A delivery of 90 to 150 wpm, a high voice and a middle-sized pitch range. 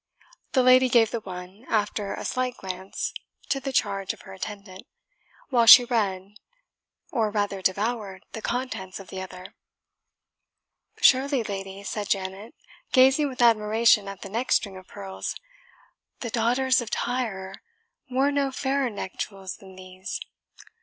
Yes: average, 145 wpm; high, 210 Hz; average, 4.6 semitones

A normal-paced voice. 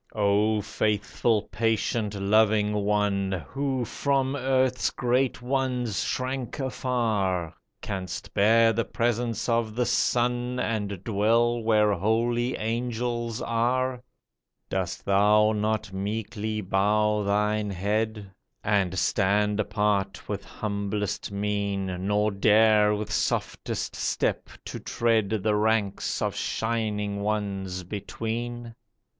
No: slow, 105 wpm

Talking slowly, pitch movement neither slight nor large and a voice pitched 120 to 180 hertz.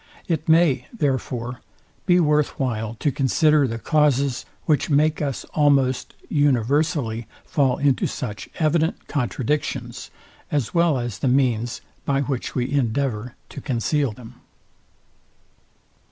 Yes: slow, 120 wpm; average, 3.6 semitones; low, 135 Hz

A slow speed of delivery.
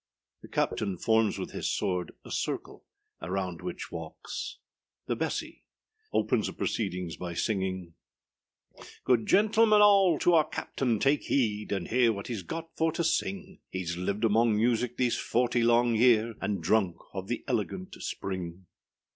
No: average, 150 wpm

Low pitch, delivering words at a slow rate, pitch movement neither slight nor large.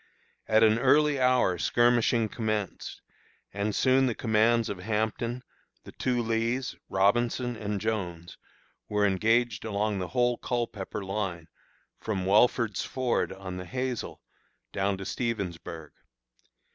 Yes: low, 110 Hz; slow, 120 wpm; average, 3.7 semitones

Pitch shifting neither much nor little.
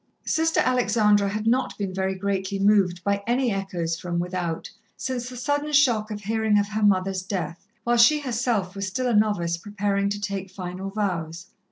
Yes: average, 3.5 semitones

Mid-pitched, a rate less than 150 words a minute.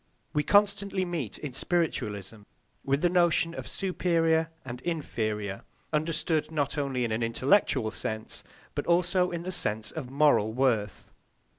Yes: medium, 150 Hz; average, 140 wpm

